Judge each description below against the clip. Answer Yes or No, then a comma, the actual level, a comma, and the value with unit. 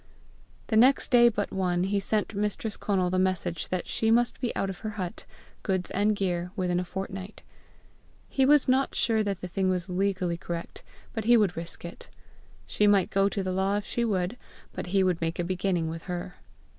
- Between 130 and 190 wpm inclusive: No, average, 200 wpm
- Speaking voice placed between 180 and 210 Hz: Yes, high, 190 Hz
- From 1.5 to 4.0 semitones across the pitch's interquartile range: Yes, average, 2.9 semitones